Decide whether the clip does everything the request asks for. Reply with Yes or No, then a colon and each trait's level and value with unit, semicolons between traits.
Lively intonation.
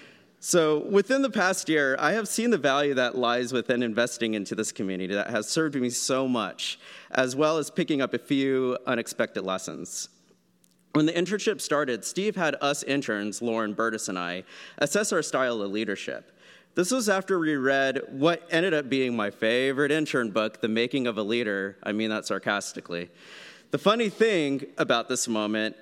Yes: wide, 5.9 semitones